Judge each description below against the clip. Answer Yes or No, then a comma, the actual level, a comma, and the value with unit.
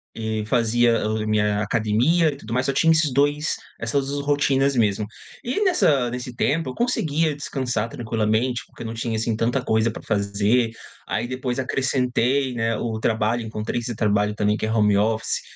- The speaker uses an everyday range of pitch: Yes, average, 3.7 semitones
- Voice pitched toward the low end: Yes, low, 120 Hz